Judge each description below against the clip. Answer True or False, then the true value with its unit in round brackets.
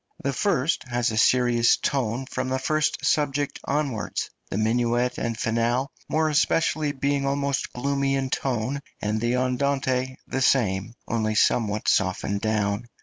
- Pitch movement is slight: False (3.3 semitones)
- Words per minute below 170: True (145 wpm)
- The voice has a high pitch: False (125 Hz)